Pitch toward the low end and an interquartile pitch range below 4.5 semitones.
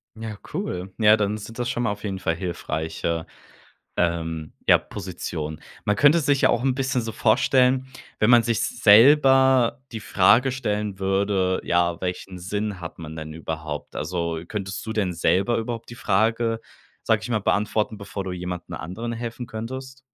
No: low, 105 Hz; average, 4.8 semitones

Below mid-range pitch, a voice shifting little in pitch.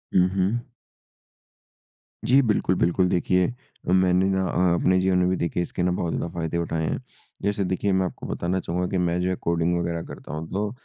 Yes: very low, 90 Hz; narrow, 1.6 semitones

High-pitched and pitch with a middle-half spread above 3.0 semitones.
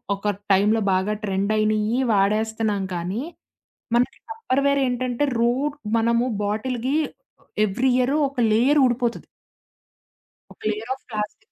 Yes: high, 230 Hz; average, 3.4 semitones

